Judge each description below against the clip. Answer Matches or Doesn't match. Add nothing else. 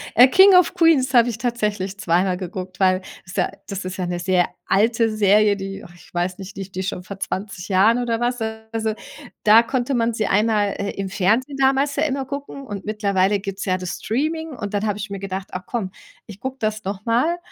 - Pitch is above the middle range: Matches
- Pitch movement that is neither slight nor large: Matches